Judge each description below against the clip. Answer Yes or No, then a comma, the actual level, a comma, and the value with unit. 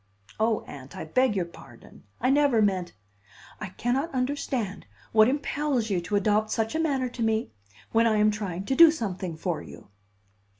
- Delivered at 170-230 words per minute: Yes, average, 180 wpm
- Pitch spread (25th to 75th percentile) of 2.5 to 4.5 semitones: No, average, 5.2 semitones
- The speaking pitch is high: Yes, high, 220 Hz